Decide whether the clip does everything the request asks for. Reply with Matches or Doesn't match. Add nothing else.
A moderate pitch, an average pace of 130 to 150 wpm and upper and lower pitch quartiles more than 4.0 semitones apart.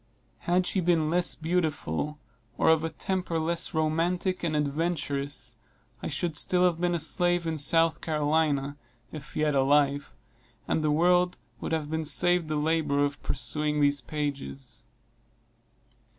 Doesn't match